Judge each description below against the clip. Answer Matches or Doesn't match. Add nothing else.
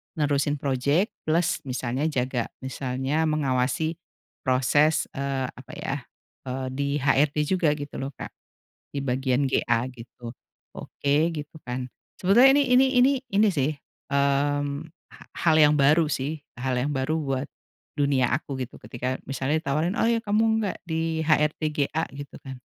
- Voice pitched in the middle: Matches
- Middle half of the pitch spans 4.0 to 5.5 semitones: Doesn't match